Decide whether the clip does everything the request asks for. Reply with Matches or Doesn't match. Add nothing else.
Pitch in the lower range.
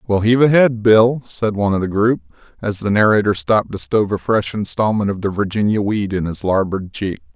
Matches